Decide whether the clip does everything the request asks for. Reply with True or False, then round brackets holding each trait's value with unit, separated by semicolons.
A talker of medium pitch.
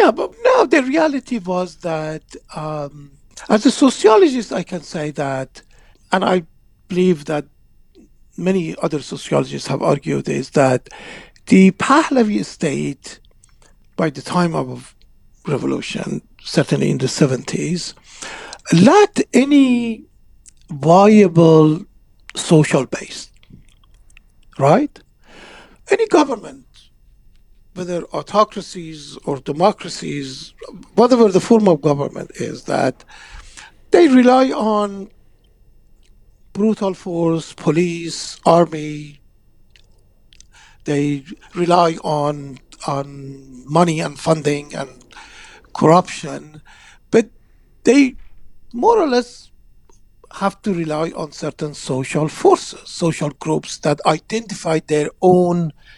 True (170 Hz)